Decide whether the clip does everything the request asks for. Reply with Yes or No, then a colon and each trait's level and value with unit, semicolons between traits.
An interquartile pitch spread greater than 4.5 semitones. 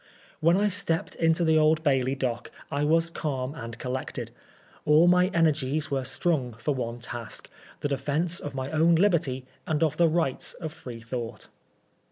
No: average, 4.1 semitones